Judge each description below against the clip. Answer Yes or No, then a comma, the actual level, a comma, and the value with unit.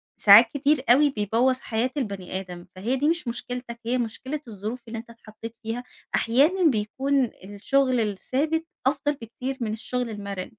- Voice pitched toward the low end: No, high, 235 Hz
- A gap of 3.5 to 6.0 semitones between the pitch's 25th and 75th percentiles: Yes, average, 3.8 semitones